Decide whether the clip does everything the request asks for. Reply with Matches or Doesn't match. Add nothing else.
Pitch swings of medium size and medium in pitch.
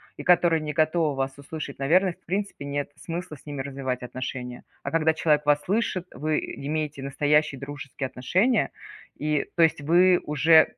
Matches